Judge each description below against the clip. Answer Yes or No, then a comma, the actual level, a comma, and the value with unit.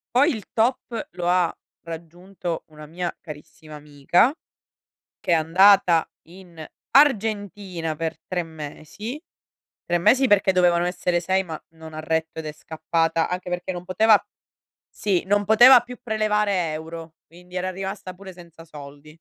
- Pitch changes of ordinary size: Yes, average, 3.7 semitones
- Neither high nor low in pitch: Yes, medium, 180 Hz